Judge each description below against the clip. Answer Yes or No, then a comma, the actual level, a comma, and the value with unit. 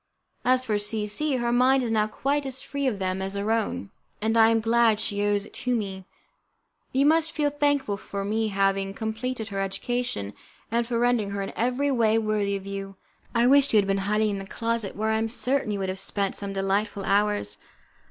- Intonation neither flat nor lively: Yes, average, 3.6 semitones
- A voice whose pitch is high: Yes, high, 215 Hz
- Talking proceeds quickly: Yes, fast, 220 wpm